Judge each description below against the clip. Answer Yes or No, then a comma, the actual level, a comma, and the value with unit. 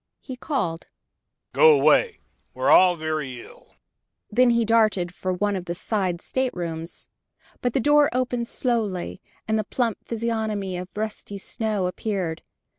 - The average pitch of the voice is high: Yes, high, 210 Hz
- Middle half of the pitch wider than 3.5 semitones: Yes, average, 4.7 semitones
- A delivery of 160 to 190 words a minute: No, average, 140 wpm